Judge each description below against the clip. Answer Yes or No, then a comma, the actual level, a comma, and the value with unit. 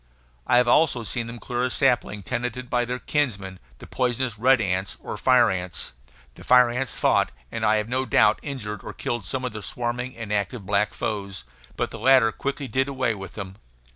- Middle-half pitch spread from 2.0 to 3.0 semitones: No, average, 3.4 semitones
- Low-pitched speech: Yes, low, 120 Hz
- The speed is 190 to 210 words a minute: Yes, average, 200 wpm